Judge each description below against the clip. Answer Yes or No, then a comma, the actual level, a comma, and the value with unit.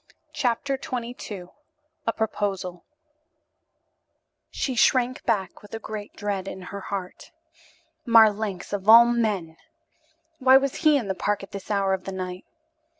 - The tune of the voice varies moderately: Yes, average, 3.7 semitones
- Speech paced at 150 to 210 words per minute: No, average, 140 wpm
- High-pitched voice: Yes, high, 210 Hz